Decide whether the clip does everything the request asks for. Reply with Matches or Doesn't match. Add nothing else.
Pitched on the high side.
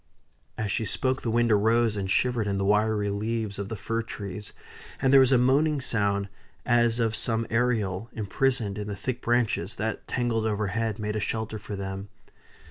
Doesn't match